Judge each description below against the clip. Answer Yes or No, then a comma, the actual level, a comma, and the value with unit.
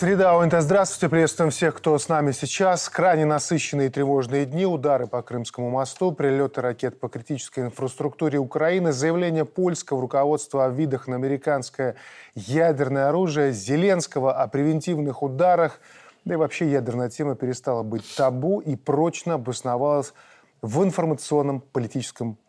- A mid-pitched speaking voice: Yes, medium, 145 Hz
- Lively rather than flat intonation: No, average, 3.6 semitones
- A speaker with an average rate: Yes, average, 135 wpm